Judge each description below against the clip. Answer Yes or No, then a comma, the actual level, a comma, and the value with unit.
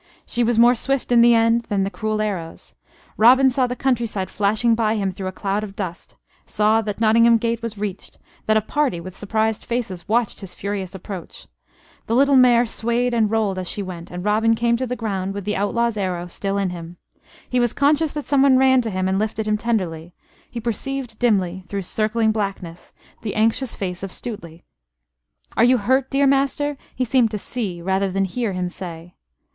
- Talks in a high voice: Yes, high, 215 Hz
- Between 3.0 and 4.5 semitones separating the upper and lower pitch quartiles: Yes, average, 3.7 semitones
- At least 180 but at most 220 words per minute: Yes, average, 200 wpm